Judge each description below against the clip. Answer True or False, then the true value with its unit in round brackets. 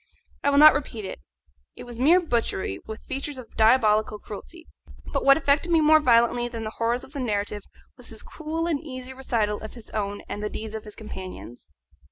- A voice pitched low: False (240 Hz)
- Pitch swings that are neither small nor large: True (4.9 semitones)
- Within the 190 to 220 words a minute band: True (205 wpm)